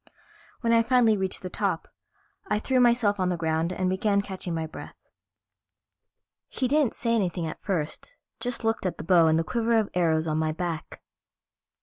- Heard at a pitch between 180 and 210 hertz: Yes, high, 190 Hz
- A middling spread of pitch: No, wide, 5.7 semitones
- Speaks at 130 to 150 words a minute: No, average, 185 wpm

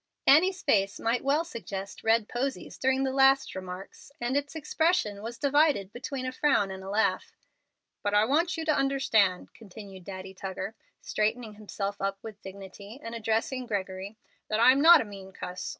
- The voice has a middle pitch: No, high, 225 Hz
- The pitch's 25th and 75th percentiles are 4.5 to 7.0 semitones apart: Yes, wide, 5.5 semitones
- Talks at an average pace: Yes, average, 170 wpm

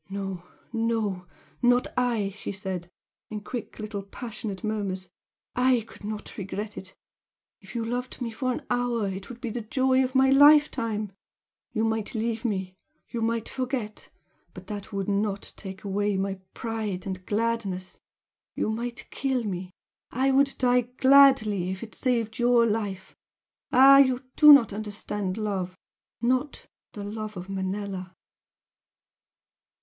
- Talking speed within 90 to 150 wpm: Yes, average, 145 wpm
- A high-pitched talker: Yes, high, 220 Hz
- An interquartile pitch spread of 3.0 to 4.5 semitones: Yes, average, 3.8 semitones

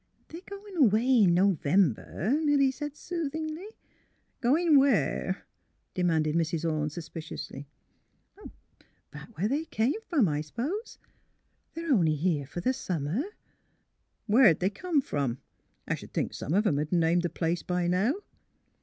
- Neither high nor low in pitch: No, high, 200 Hz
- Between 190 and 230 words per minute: No, average, 165 wpm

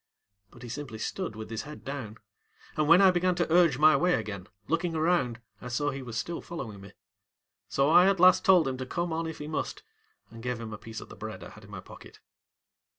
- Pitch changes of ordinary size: No, wide, 6.6 semitones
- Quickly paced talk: Yes, fast, 240 wpm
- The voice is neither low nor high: Yes, medium, 145 Hz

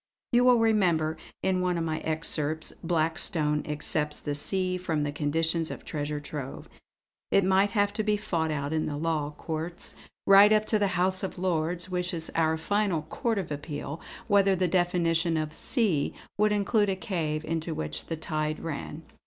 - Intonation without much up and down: No, average, 3.6 semitones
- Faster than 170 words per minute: Yes, average, 180 wpm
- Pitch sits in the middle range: Yes, medium, 165 Hz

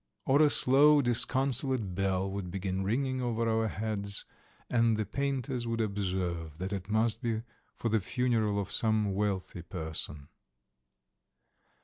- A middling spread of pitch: Yes, average, 4.0 semitones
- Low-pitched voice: Yes, low, 110 Hz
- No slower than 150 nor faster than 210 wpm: No, slow, 135 wpm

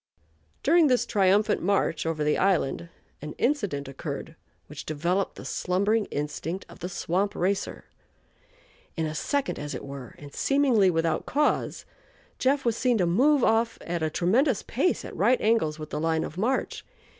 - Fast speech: No, average, 165 wpm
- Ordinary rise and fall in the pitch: No, wide, 6.9 semitones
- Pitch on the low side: No, medium, 185 Hz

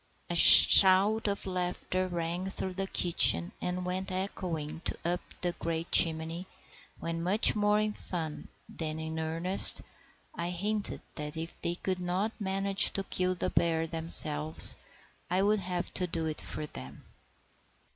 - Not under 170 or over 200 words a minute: No, average, 150 wpm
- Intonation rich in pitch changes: No, average, 2.7 semitones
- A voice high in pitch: No, medium, 180 Hz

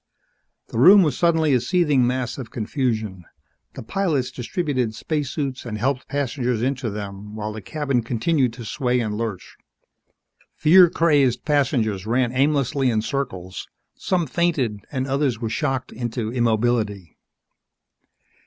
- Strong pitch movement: No, average, 4.4 semitones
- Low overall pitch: Yes, low, 125 Hz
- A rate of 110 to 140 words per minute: Yes, slow, 135 wpm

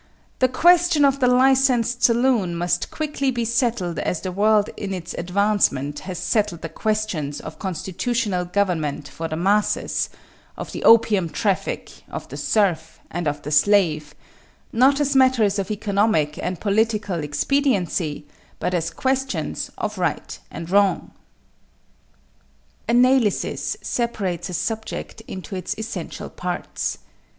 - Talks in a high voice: Yes, high, 205 Hz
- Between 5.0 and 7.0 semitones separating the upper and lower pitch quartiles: Yes, wide, 5.6 semitones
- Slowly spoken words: Yes, slow, 130 wpm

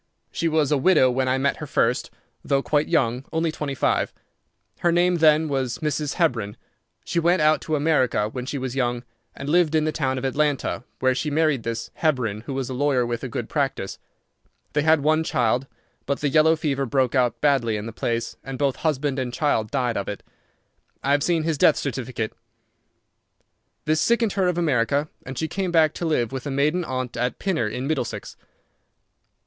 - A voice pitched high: No, medium, 140 Hz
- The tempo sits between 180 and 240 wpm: Yes, average, 195 wpm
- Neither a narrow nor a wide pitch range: Yes, average, 3.8 semitones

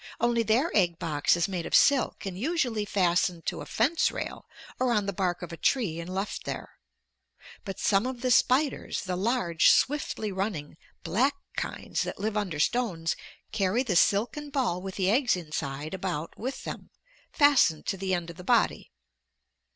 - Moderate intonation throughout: No, wide, 5.7 semitones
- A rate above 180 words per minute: No, average, 175 wpm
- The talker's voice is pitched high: Yes, high, 195 Hz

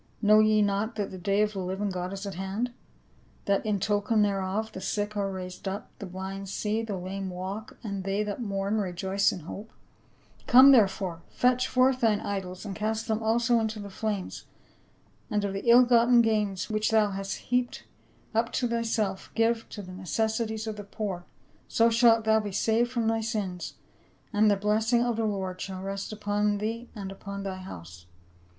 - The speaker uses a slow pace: No, average, 190 wpm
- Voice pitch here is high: Yes, high, 210 Hz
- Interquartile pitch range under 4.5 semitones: Yes, narrow, 2.4 semitones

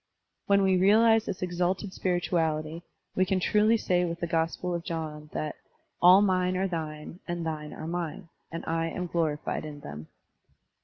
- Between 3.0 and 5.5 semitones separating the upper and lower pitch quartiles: No, narrow, 2.6 semitones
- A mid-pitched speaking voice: Yes, medium, 175 Hz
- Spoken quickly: No, average, 165 wpm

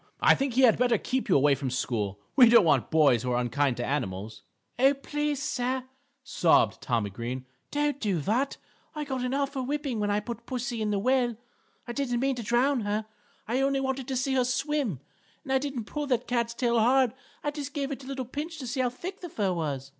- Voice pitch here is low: No, high, 245 Hz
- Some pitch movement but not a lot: No, wide, 5.9 semitones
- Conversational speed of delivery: No, fast, 225 wpm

